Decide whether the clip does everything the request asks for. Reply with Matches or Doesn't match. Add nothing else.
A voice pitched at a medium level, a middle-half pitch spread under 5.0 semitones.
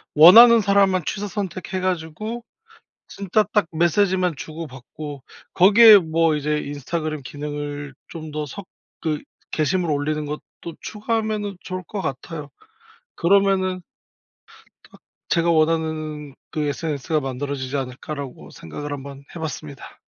Matches